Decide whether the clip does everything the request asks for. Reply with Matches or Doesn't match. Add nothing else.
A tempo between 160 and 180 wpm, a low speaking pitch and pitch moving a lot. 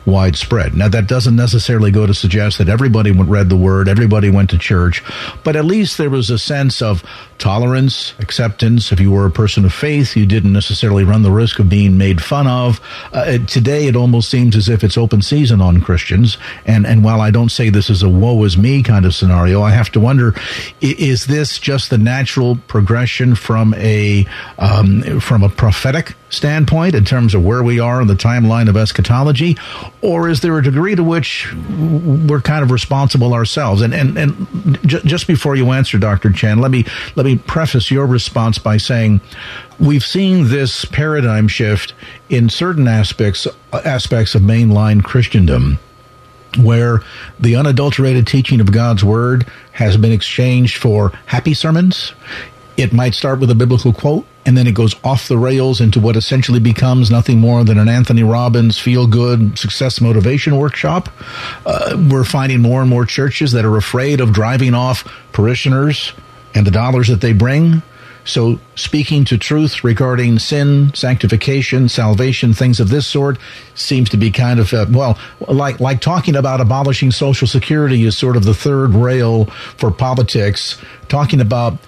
Doesn't match